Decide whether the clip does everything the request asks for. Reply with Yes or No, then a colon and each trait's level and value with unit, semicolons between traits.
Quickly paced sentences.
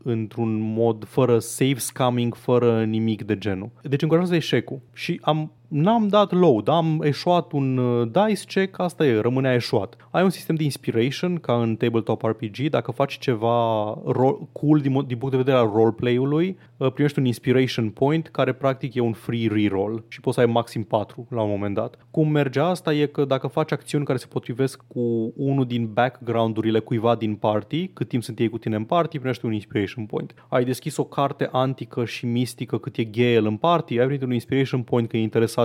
Yes: fast, 200 wpm